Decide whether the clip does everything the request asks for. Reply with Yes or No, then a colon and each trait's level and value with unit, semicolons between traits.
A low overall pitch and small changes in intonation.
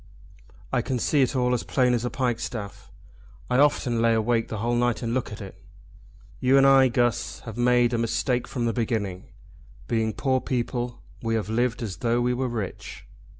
Yes: low, 120 Hz; narrow, 1.7 semitones